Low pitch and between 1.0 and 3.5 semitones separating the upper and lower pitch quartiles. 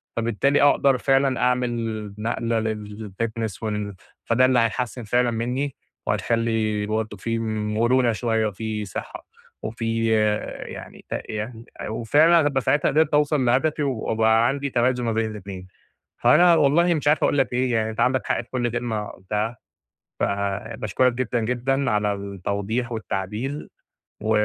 Yes: low, 115 Hz; average, 3.0 semitones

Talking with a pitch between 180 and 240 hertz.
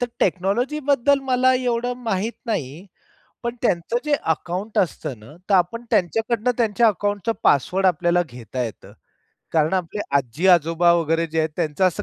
Yes: medium, 185 Hz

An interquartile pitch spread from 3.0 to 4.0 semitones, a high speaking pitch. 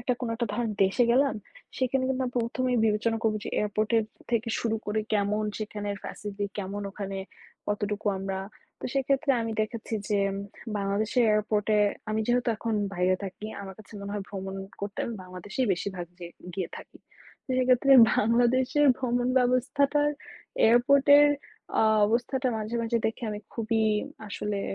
Yes: average, 3.3 semitones; high, 220 Hz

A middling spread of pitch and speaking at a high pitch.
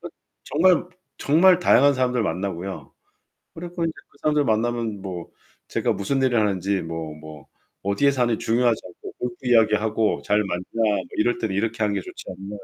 No: average, 4.6 semitones; low, 110 Hz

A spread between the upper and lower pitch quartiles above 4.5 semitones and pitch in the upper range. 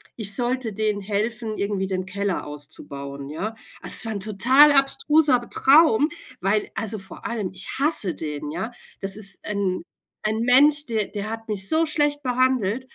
Yes: average, 4.9 semitones; high, 215 Hz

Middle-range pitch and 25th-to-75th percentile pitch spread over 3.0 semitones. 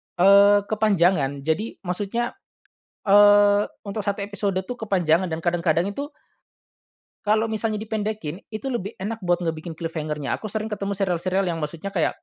No: high, 200 Hz; average, 3.7 semitones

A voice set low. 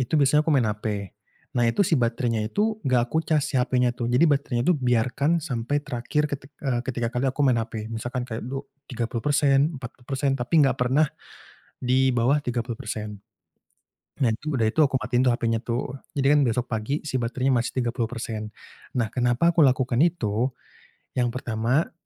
Yes: low, 125 Hz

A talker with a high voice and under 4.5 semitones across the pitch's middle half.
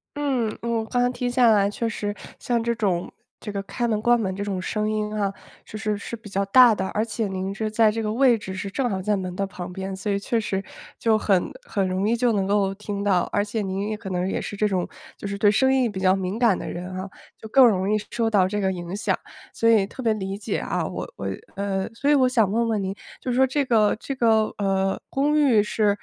Yes: high, 210 Hz; average, 3.0 semitones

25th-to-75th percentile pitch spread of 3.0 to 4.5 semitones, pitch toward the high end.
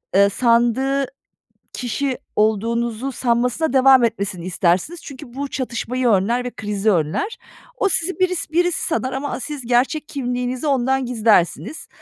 Yes: average, 3.4 semitones; very high, 250 Hz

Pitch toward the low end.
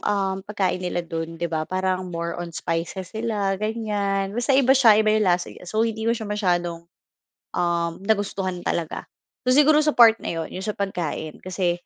No: high, 195 Hz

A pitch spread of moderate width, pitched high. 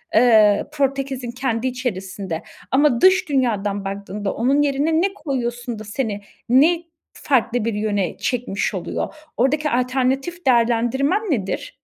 Yes: average, 4.3 semitones; very high, 250 Hz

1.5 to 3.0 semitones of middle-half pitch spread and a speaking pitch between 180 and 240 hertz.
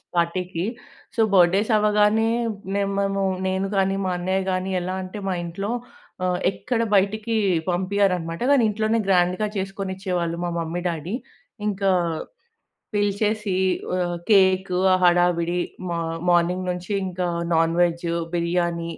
Yes: narrow, 2.4 semitones; medium, 185 Hz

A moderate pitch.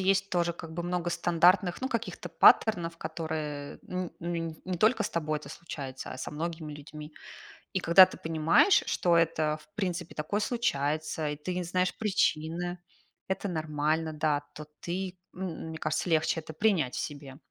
Yes: medium, 165 Hz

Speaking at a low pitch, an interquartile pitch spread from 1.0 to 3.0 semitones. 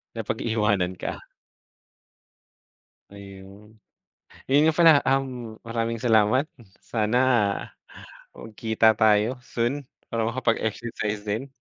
Yes: low, 110 Hz; narrow, 2.6 semitones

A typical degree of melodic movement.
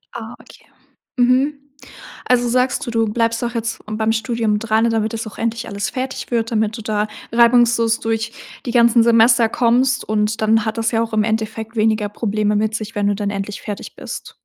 No: narrow, 1.6 semitones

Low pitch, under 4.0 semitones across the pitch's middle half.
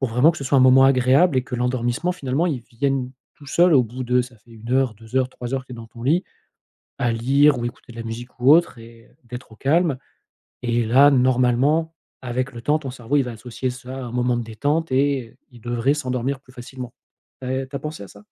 Yes: low, 130 Hz; narrow, 2.5 semitones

